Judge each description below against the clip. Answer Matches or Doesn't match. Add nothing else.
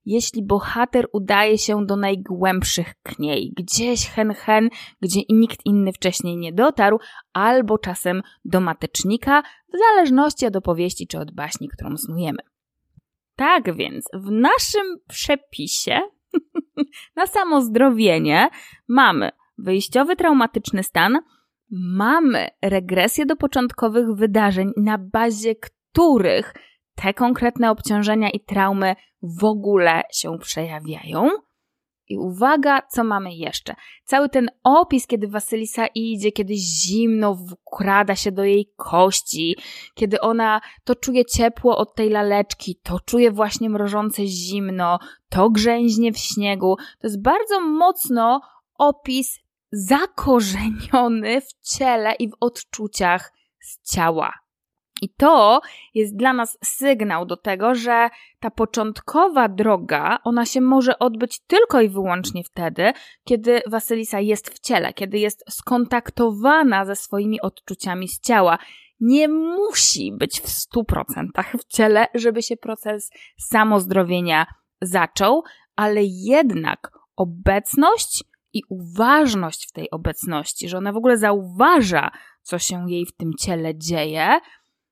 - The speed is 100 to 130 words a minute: Matches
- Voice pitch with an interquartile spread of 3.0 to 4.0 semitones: Doesn't match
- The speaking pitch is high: Matches